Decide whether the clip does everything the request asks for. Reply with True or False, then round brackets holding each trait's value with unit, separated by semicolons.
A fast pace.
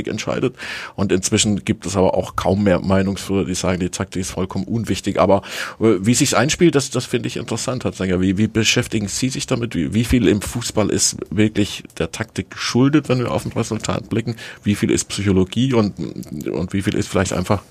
True (205 wpm)